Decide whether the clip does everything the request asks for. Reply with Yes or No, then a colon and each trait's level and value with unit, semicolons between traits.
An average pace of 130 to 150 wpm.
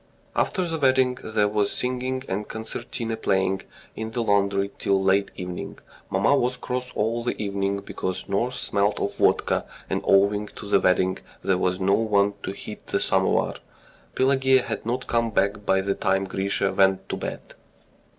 No: average, 170 wpm